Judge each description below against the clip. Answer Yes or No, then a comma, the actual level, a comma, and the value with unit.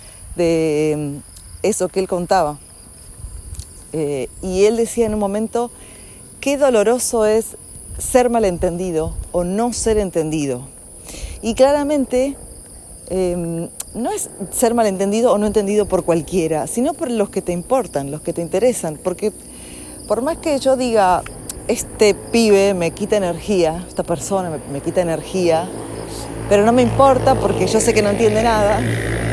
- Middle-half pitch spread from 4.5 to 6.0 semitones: Yes, wide, 5.6 semitones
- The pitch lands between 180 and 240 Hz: Yes, high, 190 Hz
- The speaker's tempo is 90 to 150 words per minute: Yes, average, 145 wpm